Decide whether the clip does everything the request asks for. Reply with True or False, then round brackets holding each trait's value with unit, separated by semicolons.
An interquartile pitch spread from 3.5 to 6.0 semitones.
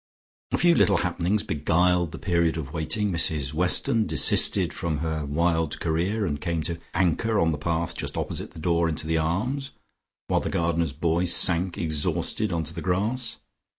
False (2.4 semitones)